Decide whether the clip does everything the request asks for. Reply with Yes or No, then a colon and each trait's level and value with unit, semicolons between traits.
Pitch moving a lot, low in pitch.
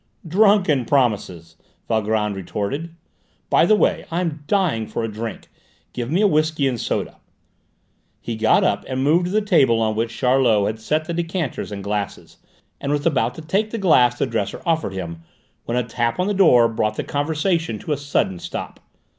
Yes: wide, 7.0 semitones; low, 130 Hz